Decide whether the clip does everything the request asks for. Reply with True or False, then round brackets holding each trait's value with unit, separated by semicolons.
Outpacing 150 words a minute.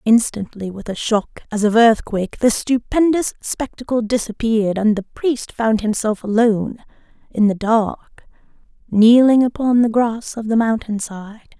False (145 wpm)